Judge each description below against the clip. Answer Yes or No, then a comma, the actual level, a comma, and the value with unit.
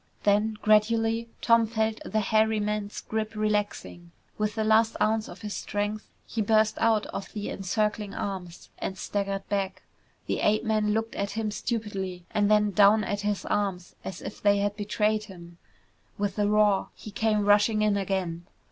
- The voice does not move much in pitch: Yes, narrow, 1.4 semitones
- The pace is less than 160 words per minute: No, average, 170 wpm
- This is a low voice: No, high, 210 Hz